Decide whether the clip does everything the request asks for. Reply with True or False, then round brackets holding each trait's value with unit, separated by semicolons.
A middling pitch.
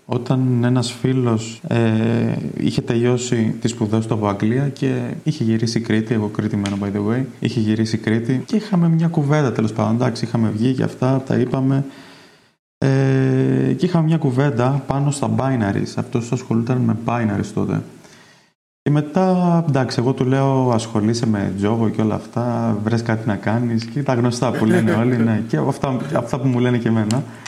False (120 Hz)